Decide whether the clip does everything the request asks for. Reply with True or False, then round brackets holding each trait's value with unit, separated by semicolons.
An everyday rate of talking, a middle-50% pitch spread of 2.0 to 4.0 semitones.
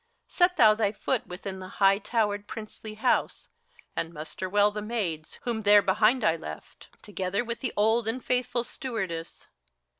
True (160 wpm; 3.4 semitones)